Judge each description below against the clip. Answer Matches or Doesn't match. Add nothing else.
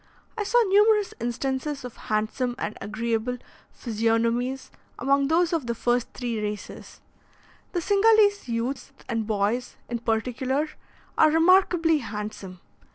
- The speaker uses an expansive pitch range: Matches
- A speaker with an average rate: Doesn't match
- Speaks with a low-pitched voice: Doesn't match